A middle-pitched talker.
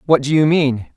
Yes: medium, 145 Hz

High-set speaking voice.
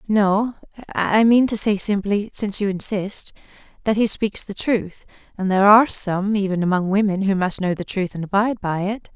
Yes: high, 200 Hz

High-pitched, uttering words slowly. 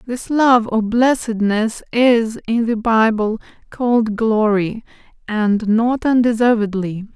Yes: high, 225 Hz; slow, 110 wpm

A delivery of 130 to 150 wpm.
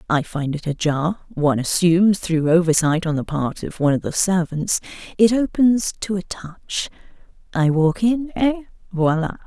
Yes: average, 145 wpm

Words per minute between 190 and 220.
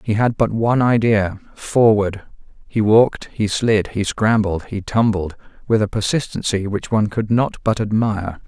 No: average, 155 wpm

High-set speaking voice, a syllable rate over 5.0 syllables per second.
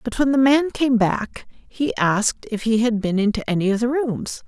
No: high, 235 Hz; 4.7 syllables/s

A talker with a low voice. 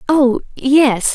No: very high, 265 Hz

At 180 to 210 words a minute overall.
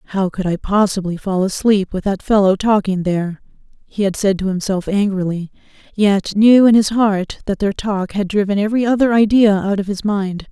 Yes: average, 195 wpm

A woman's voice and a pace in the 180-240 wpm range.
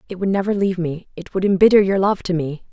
No: female; fast, 265 wpm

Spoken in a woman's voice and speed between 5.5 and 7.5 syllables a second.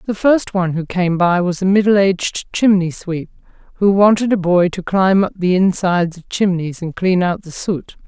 No: female; 5.0 syllables/s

